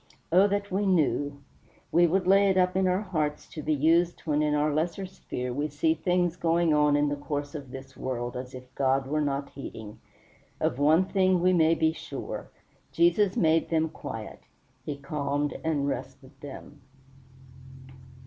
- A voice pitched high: No, medium, 155 Hz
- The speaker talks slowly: No, average, 170 wpm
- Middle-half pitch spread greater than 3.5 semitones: Yes, average, 4.0 semitones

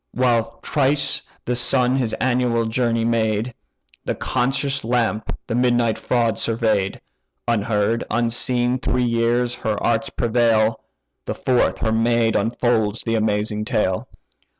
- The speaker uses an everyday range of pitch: No, narrow, 1.8 semitones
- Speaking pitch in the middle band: No, low, 115 Hz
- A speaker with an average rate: No, slow, 125 wpm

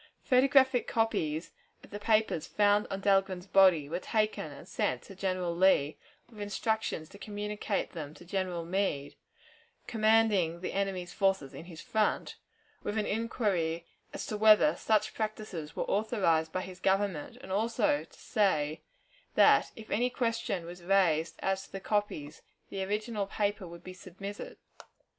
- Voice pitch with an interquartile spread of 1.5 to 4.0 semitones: Yes, average, 3.6 semitones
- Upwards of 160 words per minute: No, average, 150 wpm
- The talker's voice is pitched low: No, high, 195 Hz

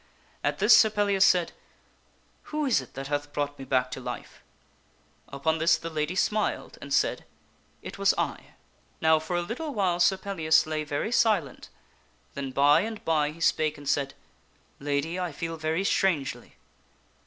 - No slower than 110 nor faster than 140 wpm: No, average, 180 wpm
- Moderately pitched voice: Yes, medium, 160 Hz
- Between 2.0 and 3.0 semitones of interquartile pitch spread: No, average, 4.6 semitones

